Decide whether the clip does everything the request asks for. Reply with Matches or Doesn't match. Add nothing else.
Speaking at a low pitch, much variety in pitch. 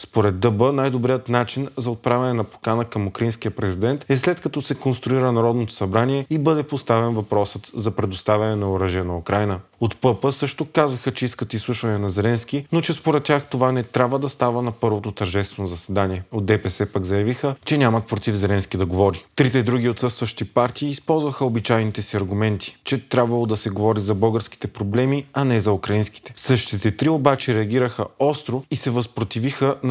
Doesn't match